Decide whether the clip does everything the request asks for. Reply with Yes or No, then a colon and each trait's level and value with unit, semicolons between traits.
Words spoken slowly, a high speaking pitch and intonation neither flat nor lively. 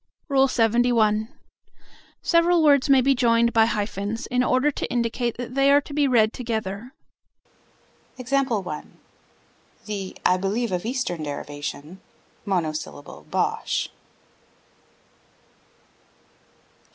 Yes: slow, 95 wpm; high, 230 Hz; average, 4.8 semitones